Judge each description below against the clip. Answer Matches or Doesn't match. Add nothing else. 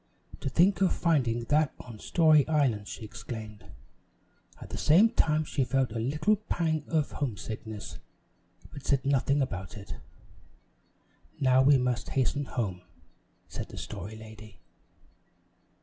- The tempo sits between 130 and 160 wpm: Matches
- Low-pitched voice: Matches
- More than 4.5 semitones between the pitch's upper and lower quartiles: Matches